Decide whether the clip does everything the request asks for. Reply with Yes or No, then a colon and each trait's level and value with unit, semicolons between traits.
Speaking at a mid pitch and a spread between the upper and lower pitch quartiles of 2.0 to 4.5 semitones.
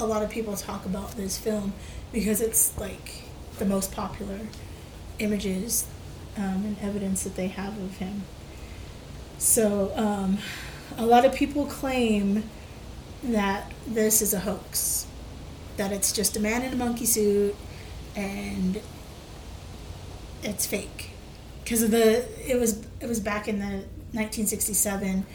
No: high, 205 Hz; narrow, 2.4 semitones